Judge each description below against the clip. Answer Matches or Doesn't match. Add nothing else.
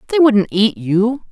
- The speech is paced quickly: Doesn't match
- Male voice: Doesn't match